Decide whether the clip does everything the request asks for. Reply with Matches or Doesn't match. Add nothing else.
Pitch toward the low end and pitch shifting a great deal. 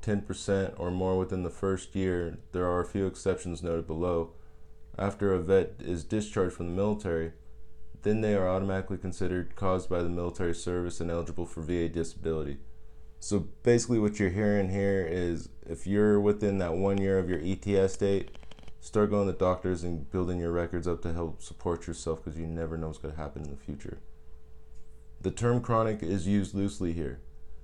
Doesn't match